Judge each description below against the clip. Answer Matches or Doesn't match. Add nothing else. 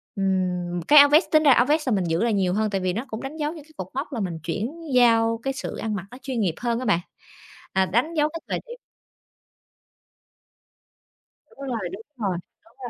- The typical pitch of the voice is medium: Doesn't match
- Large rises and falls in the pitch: Matches